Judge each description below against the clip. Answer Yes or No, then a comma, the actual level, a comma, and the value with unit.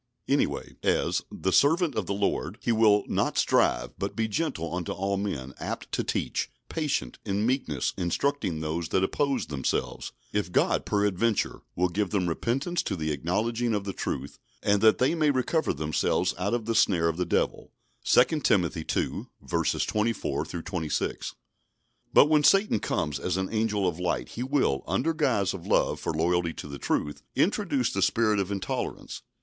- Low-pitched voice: Yes, low, 100 Hz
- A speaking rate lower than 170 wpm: No, average, 175 wpm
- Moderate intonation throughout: No, wide, 5.9 semitones